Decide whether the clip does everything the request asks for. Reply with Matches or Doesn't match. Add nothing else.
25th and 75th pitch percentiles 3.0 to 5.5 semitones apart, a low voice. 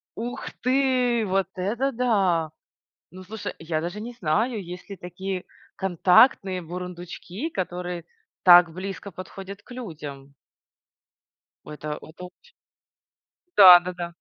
Doesn't match